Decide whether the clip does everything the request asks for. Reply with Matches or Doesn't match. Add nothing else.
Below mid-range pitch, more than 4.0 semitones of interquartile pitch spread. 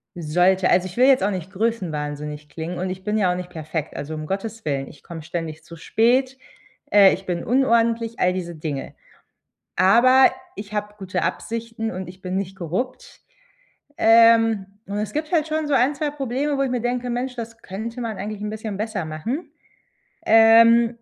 Doesn't match